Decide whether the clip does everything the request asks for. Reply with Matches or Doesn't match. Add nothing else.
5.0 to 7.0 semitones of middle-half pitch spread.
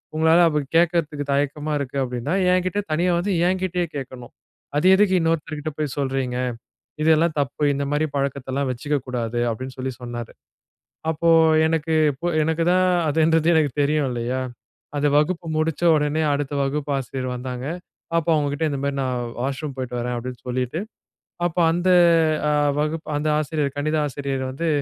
Doesn't match